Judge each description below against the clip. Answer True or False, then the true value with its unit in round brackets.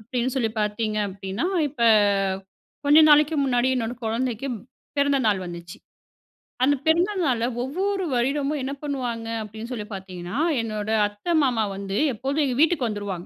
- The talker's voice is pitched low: False (240 Hz)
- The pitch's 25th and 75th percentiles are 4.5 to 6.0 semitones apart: True (5.0 semitones)